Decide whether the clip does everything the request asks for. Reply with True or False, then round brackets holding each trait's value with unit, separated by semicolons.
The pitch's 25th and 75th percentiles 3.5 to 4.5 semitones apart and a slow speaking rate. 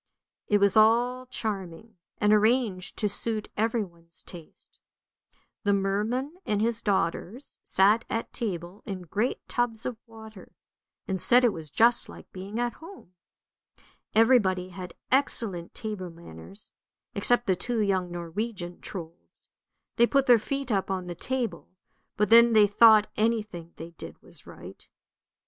False (4.1 semitones; 145 wpm)